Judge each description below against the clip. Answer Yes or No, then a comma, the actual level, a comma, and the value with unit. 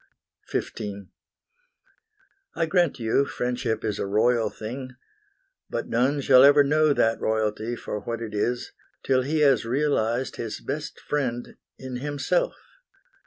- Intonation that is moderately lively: Yes, average, 4.0 semitones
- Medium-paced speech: No, slow, 130 wpm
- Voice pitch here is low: Yes, low, 125 Hz